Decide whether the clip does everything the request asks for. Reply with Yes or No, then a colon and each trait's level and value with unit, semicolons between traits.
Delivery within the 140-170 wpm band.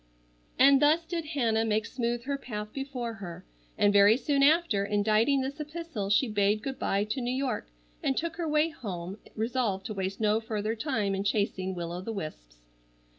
No: average, 185 wpm